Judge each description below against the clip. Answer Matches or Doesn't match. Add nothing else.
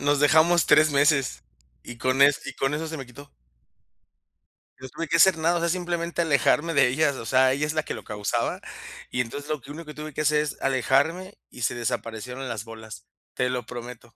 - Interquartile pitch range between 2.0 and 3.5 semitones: Doesn't match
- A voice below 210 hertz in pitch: Matches